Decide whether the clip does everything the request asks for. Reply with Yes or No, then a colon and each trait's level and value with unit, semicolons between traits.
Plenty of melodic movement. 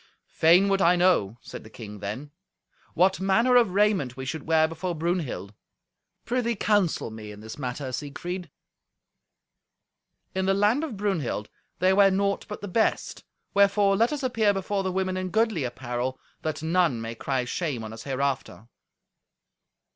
Yes: wide, 7.4 semitones